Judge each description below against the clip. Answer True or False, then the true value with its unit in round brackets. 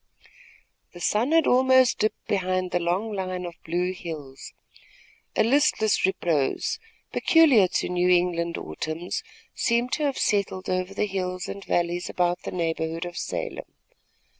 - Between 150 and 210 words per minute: False (140 wpm)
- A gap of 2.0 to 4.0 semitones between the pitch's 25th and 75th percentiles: True (3.6 semitones)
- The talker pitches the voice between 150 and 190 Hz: True (185 Hz)